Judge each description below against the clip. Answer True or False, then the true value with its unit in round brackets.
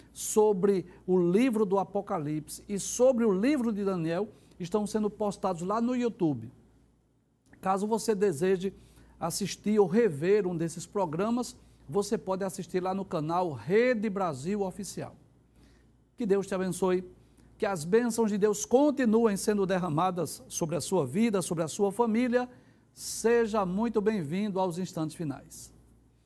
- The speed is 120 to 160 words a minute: True (140 wpm)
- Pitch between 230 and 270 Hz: False (195 Hz)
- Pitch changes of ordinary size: True (3.8 semitones)